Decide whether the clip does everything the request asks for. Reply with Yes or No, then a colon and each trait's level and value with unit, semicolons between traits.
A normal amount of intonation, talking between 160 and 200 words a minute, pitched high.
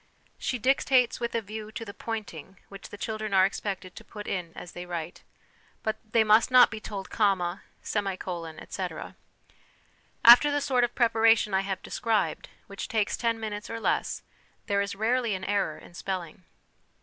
Yes: average, 3.0 semitones; average, 175 wpm; high, 210 Hz